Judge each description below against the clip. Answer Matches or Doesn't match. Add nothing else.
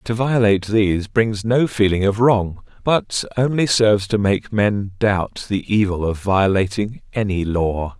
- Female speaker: Doesn't match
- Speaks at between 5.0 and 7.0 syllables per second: Doesn't match